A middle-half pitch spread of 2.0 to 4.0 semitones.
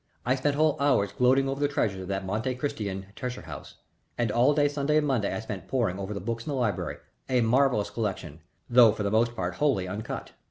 No: average, 5.2 semitones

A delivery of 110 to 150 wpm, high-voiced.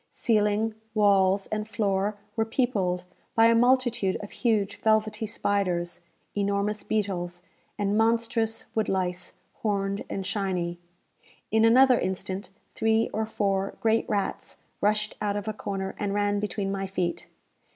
Yes: average, 140 wpm; high, 205 Hz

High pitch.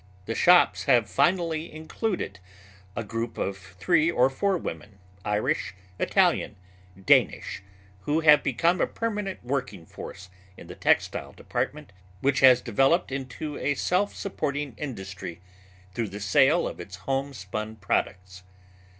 No: low, 130 Hz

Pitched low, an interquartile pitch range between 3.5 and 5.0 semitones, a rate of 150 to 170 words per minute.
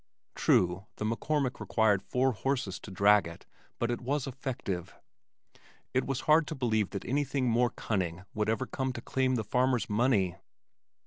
Yes: low, 120 Hz; average, 4.2 semitones; average, 165 wpm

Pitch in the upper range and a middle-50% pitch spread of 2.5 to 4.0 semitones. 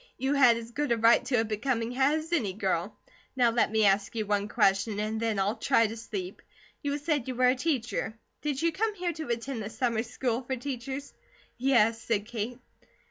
Yes: high, 235 Hz; average, 3.7 semitones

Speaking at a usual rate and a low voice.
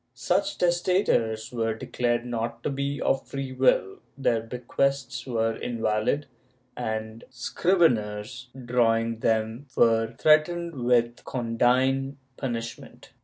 No: slow, 110 wpm; low, 120 Hz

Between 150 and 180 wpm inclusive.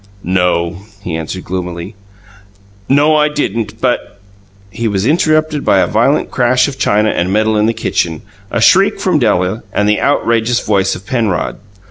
Yes: average, 165 wpm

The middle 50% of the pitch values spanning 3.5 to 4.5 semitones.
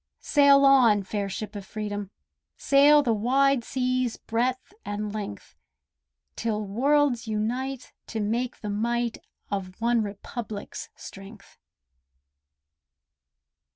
Yes: average, 3.8 semitones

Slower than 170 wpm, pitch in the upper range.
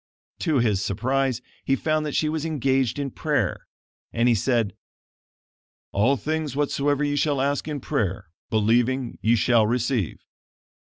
No: average, 145 wpm; low, 130 Hz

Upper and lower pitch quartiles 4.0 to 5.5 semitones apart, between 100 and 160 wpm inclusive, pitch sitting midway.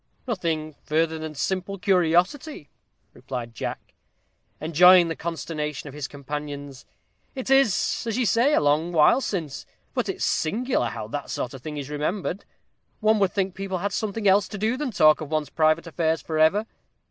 No: average, 4.9 semitones; average, 170 wpm; medium, 165 Hz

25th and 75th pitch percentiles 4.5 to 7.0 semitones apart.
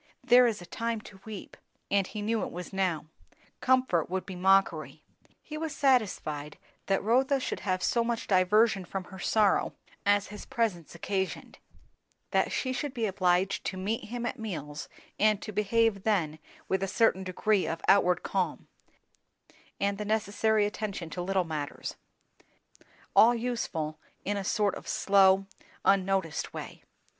No: average, 3.2 semitones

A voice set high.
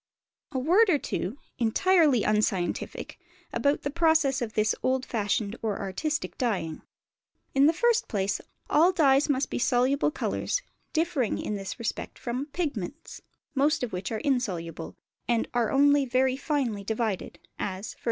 Yes: very high, 255 Hz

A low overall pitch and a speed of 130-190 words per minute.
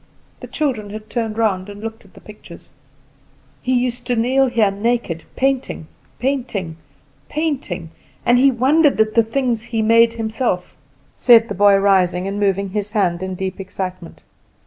No: high, 220 Hz; average, 160 wpm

